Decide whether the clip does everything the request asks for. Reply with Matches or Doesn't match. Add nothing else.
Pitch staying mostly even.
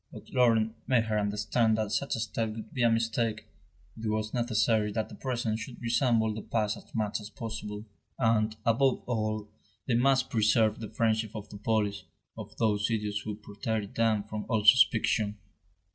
Matches